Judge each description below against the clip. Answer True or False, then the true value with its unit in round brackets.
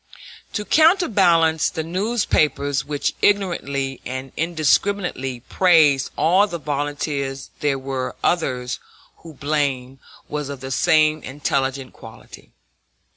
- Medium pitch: True (145 Hz)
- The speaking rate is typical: False (115 wpm)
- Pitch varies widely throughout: False (4.2 semitones)